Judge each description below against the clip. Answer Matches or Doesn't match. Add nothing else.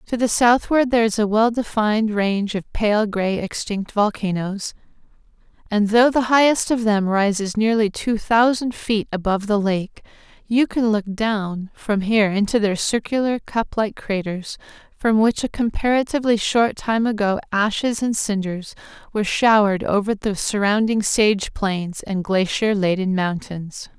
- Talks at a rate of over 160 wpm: Doesn't match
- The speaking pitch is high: Matches